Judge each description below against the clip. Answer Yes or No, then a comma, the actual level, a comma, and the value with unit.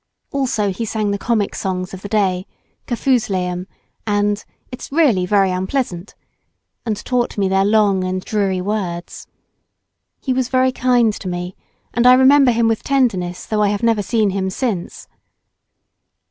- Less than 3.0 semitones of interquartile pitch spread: No, average, 4.2 semitones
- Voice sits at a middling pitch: No, high, 205 Hz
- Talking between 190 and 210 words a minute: No, average, 155 wpm